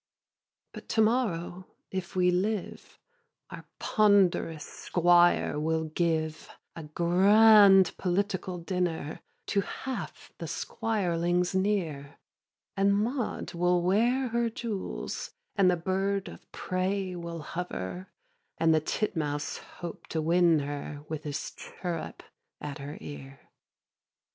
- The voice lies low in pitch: No, medium, 180 Hz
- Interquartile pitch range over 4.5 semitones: No, average, 3.7 semitones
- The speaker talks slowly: Yes, slow, 115 wpm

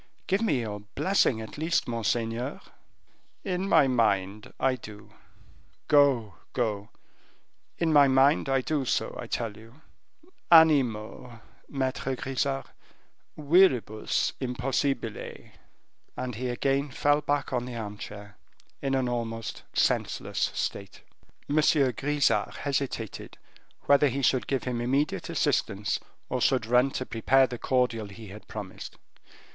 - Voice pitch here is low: Yes, low, 125 Hz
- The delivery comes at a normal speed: No, slow, 125 wpm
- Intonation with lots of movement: No, average, 3.7 semitones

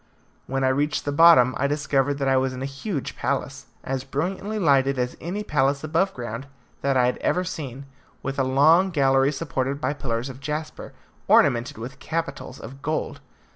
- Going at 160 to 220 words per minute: Yes, average, 180 wpm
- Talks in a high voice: No, medium, 140 Hz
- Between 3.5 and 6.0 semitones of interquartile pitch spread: No, average, 2.8 semitones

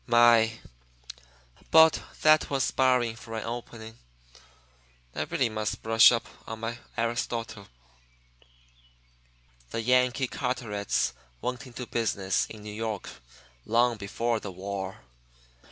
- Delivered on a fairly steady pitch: Yes, narrow, 2.2 semitones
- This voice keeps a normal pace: No, slow, 110 wpm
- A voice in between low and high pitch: No, low, 115 Hz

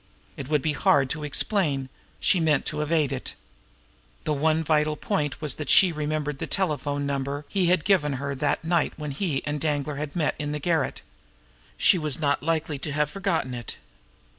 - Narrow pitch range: Yes, narrow, 2.0 semitones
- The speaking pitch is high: No, medium, 150 Hz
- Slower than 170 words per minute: No, average, 190 wpm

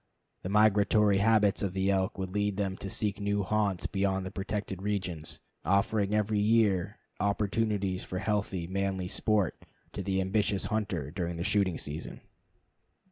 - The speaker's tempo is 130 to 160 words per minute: Yes, average, 150 wpm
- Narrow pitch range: Yes, narrow, 1.8 semitones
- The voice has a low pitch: Yes, low, 100 Hz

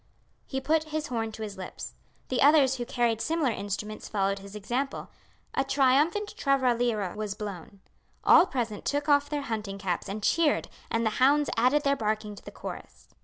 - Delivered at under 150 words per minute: No, average, 175 wpm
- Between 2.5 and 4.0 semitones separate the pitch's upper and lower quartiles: No, average, 5.3 semitones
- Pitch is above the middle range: Yes, high, 240 Hz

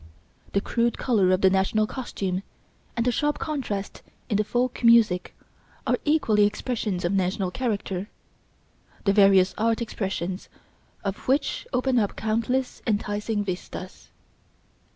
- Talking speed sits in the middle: No, slow, 130 wpm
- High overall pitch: Yes, high, 210 Hz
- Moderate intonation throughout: Yes, average, 3.6 semitones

